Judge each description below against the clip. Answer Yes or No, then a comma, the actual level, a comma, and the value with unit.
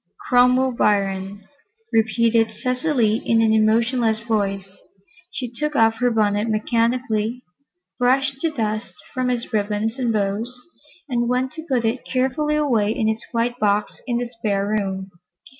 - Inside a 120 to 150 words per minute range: Yes, average, 140 wpm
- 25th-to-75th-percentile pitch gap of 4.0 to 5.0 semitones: No, average, 2.7 semitones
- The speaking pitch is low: No, high, 230 Hz